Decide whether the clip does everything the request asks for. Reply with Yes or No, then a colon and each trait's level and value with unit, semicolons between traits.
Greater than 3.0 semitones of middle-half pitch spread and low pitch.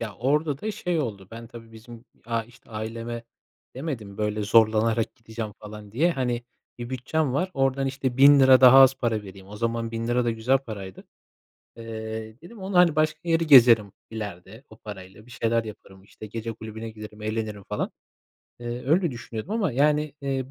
Yes: average, 3.6 semitones; low, 115 Hz